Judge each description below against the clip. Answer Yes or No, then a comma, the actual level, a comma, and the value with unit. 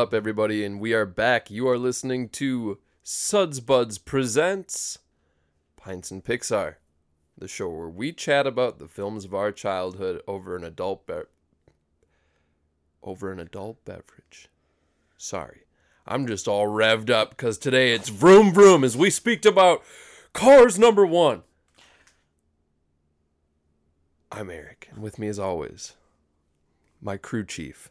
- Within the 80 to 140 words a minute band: Yes, slow, 135 wpm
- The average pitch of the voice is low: Yes, low, 100 Hz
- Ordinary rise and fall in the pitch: No, wide, 8.9 semitones